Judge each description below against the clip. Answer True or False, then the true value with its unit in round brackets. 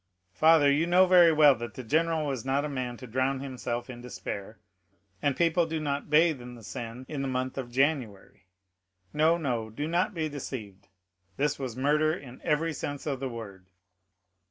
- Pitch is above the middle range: False (135 Hz)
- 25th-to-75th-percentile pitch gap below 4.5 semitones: True (4.0 semitones)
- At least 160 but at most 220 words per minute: True (185 wpm)